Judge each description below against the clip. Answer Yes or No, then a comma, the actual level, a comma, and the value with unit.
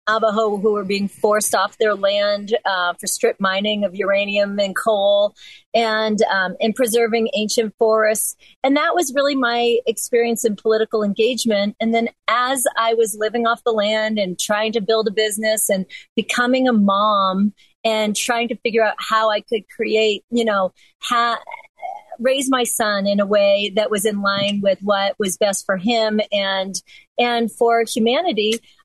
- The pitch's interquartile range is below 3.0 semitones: Yes, narrow, 2.4 semitones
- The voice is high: Yes, high, 220 Hz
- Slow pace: No, average, 170 wpm